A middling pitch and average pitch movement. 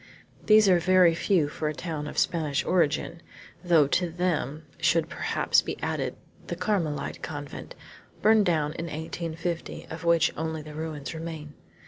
No: medium, 165 Hz; narrow, 2.3 semitones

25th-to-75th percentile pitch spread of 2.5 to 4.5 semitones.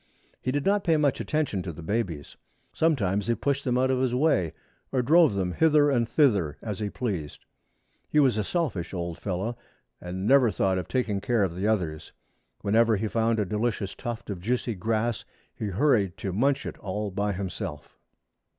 No: average, 5.3 semitones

